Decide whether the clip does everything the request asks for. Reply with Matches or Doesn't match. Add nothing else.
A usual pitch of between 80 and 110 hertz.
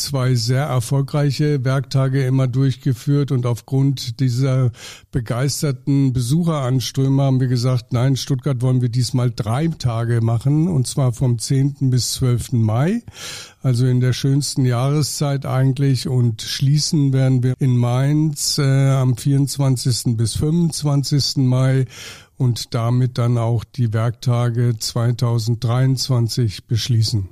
Doesn't match